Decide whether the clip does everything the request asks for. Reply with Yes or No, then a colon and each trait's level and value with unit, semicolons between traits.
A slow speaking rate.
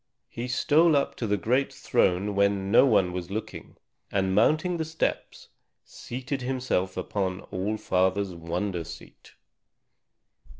Yes: slow, 130 wpm